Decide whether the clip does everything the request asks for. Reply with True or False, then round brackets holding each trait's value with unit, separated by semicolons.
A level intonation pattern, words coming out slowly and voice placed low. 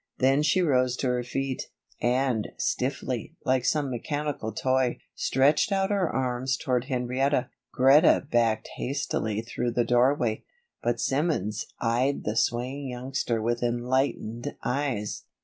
True (2.3 semitones; 130 wpm; 125 Hz)